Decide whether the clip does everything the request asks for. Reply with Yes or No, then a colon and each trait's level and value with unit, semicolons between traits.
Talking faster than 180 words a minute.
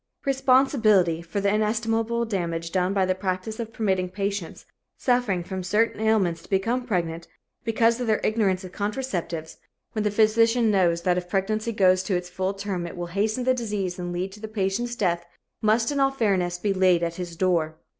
Yes: average, 190 wpm